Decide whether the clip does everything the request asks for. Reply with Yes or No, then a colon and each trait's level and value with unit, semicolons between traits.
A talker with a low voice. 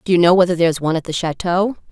No: medium, 175 Hz